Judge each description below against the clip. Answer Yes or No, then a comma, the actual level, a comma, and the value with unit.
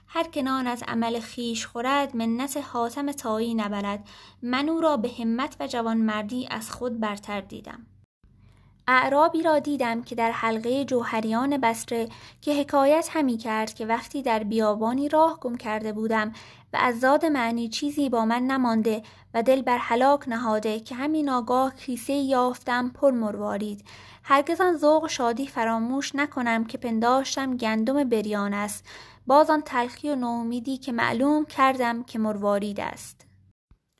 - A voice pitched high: Yes, high, 245 Hz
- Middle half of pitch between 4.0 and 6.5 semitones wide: No, average, 3.4 semitones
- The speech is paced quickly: No, average, 145 wpm